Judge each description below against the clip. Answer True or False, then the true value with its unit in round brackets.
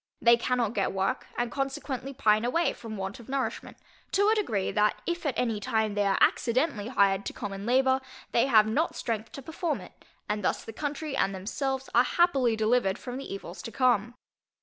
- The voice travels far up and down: False (4.3 semitones)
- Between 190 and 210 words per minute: True (195 wpm)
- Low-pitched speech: False (240 Hz)